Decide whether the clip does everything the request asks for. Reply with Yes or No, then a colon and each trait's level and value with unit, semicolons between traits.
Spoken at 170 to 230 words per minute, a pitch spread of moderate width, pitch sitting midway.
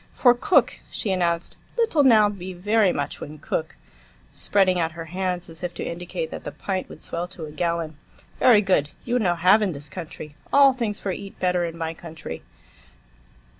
Yes: average, 190 wpm; average, 3.8 semitones; medium, 180 Hz